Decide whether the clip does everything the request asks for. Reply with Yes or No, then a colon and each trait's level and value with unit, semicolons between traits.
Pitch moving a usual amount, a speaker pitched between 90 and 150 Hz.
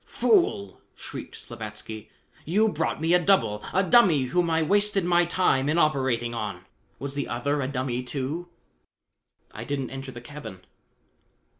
No: wide, 6.3 semitones; medium, 140 Hz